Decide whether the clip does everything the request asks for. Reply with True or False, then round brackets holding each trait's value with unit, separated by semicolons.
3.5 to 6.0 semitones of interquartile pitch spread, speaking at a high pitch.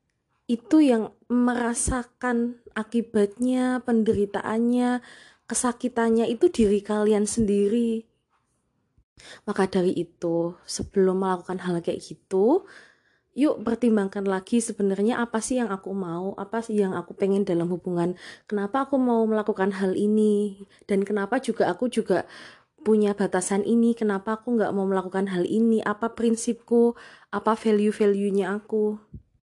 False (3.0 semitones; 215 Hz)